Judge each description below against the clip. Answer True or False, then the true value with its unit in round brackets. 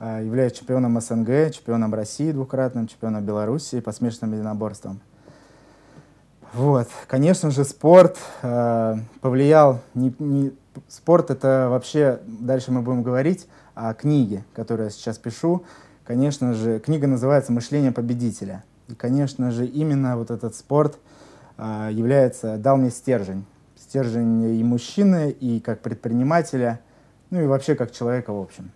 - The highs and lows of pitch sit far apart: False (3.4 semitones)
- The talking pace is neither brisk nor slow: True (130 wpm)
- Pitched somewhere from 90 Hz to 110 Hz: False (125 Hz)